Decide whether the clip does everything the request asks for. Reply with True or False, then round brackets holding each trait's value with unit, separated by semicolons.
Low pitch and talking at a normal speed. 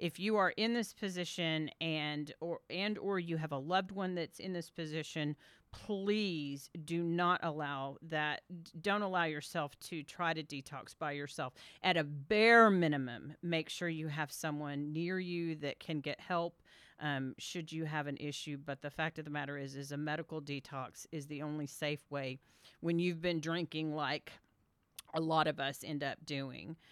False (155 Hz; 185 wpm)